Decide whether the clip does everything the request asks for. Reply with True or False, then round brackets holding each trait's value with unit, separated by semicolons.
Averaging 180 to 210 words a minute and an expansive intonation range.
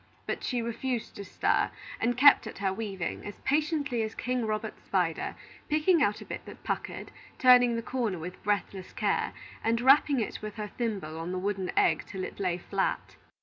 False (190 wpm; 4.5 semitones)